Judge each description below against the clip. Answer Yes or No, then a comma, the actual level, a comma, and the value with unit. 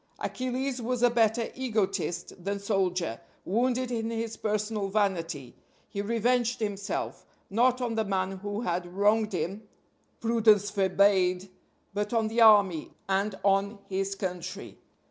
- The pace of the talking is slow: Yes, slow, 130 wpm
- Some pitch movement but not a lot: Yes, average, 3.0 semitones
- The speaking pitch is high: Yes, high, 205 Hz